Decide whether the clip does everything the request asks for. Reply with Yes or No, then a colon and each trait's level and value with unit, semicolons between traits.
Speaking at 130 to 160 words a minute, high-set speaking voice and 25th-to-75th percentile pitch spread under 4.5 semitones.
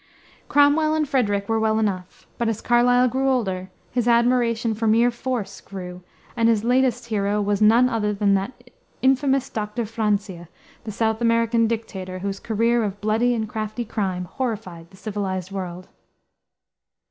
Yes: average, 155 wpm; high, 220 Hz; average, 3.2 semitones